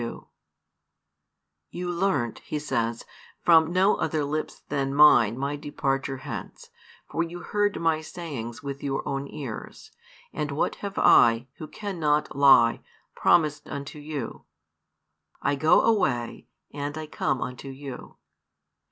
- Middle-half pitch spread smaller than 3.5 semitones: Yes, average, 2.9 semitones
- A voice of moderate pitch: Yes, medium, 145 Hz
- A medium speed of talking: No, slow, 130 wpm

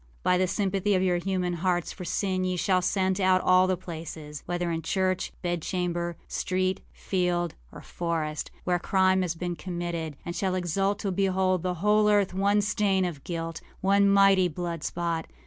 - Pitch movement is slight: Yes, narrow, 1.7 semitones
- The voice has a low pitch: No, medium, 185 Hz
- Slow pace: No, average, 165 wpm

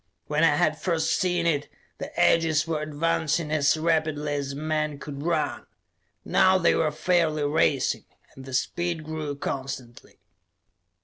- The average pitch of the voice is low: No, medium, 155 Hz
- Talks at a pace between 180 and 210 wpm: No, average, 145 wpm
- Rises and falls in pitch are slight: Yes, narrow, 2.1 semitones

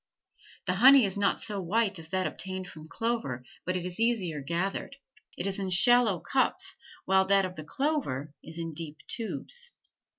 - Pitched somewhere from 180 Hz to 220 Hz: Yes, high, 190 Hz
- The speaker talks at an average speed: Yes, average, 175 wpm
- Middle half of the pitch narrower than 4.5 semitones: No, average, 5.3 semitones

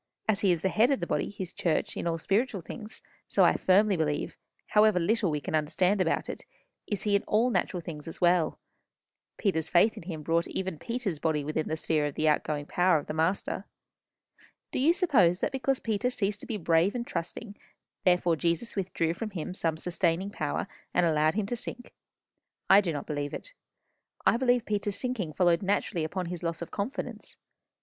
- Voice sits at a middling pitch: Yes, medium, 180 Hz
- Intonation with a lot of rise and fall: No, average, 4.6 semitones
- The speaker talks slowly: No, average, 200 wpm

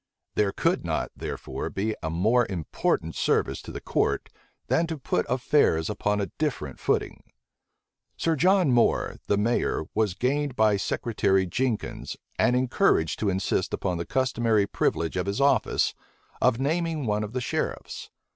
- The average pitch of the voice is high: No, low, 110 Hz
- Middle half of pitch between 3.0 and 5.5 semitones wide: Yes, average, 5.2 semitones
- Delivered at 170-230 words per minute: No, average, 155 wpm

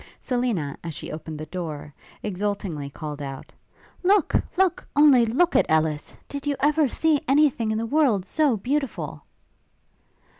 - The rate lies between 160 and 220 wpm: No, average, 150 wpm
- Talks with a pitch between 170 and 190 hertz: No, high, 225 Hz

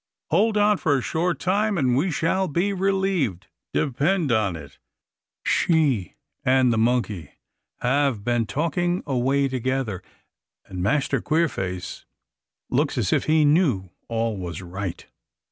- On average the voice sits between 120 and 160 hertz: Yes, low, 135 Hz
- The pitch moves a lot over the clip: Yes, wide, 7.3 semitones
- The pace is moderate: No, slow, 130 wpm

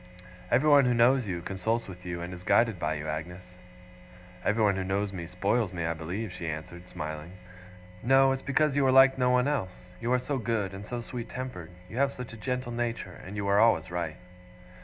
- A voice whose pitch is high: No, low, 105 Hz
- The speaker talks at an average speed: No, fast, 210 wpm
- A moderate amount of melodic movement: No, wide, 5.9 semitones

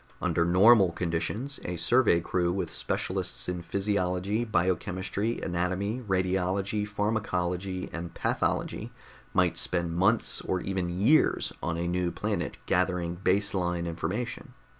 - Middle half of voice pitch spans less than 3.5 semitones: Yes, average, 2.8 semitones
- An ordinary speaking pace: No, slow, 120 wpm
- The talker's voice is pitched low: Yes, very low, 95 Hz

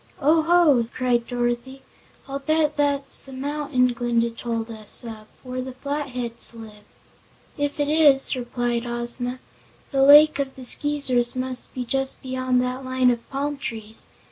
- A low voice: No, very high, 255 Hz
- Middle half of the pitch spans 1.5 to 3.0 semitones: Yes, average, 2.7 semitones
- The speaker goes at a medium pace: Yes, average, 150 wpm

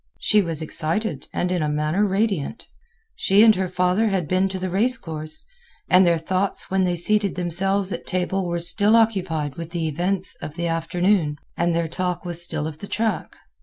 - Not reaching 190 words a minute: No, average, 195 wpm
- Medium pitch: Yes, medium, 180 Hz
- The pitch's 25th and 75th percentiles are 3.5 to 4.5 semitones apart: No, average, 2.9 semitones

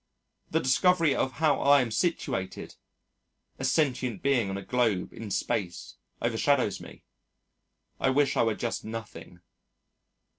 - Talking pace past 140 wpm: No, slow, 135 wpm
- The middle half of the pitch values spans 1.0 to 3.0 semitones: No, average, 4.6 semitones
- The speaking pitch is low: Yes, low, 125 Hz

